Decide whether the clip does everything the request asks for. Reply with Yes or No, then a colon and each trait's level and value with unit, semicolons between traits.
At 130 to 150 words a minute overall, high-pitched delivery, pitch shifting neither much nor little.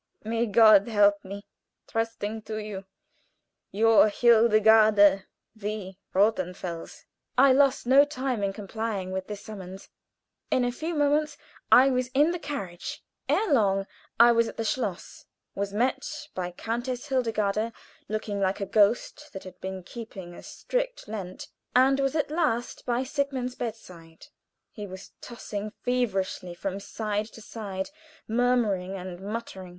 Yes: average, 140 wpm; high, 220 Hz; average, 4.1 semitones